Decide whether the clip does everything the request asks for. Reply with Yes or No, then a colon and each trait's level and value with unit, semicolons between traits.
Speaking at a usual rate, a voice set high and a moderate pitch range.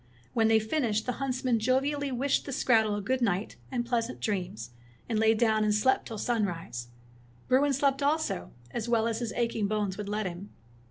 Yes: average, 185 wpm; high, 225 Hz; average, 3.5 semitones